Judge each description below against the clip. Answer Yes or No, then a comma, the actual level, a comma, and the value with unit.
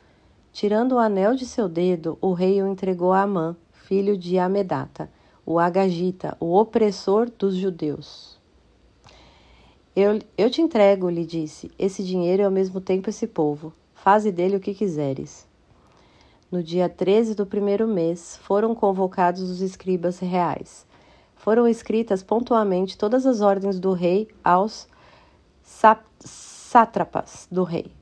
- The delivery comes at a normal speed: Yes, average, 135 wpm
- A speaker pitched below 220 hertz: Yes, high, 190 Hz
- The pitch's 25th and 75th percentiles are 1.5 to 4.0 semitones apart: Yes, average, 2.8 semitones